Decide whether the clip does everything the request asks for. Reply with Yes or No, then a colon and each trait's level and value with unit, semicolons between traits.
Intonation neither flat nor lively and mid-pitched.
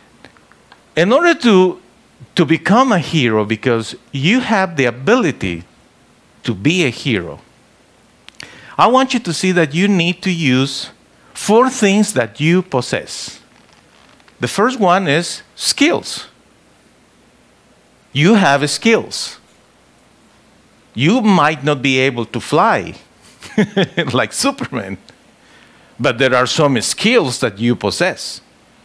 No: wide, 8.0 semitones; medium, 155 Hz